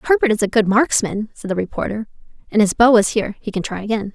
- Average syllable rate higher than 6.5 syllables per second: Yes, 6.7 syllables/s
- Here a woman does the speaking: Yes, female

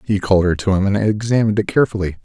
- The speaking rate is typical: No, fast, 240 wpm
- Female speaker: No, male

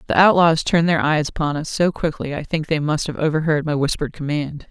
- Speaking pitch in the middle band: Yes, medium, 155 Hz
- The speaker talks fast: Yes, fast, 230 wpm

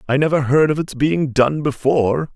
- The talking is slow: No, fast, 205 wpm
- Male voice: Yes, male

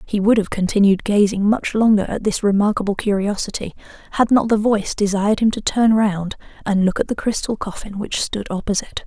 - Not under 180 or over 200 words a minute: Yes, average, 190 wpm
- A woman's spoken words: Yes, female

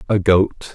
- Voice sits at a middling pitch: No, very low, 95 Hz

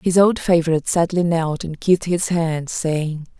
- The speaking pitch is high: No, medium, 165 Hz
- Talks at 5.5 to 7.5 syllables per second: No, 4.7 syllables/s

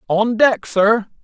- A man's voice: Yes, male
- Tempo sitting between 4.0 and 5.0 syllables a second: No, 3.3 syllables/s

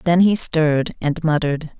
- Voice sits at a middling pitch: Yes, medium, 160 Hz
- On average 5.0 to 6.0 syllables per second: Yes, 5.1 syllables/s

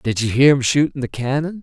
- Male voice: Yes, male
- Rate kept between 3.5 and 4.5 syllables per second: No, 5.7 syllables/s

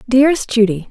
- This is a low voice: No, high, 235 Hz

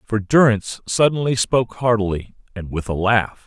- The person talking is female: No, male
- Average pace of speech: Yes, average, 155 wpm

